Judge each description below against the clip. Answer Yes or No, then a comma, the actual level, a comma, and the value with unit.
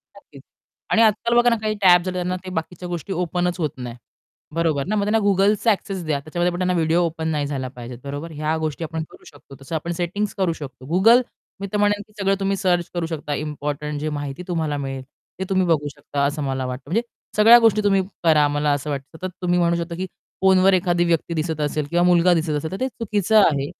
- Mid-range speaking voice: Yes, medium, 170 Hz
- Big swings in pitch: No, average, 4.2 semitones